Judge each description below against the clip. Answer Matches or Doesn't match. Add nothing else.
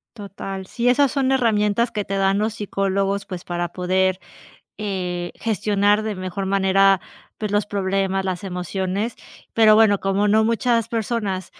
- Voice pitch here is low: Doesn't match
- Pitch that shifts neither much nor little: Doesn't match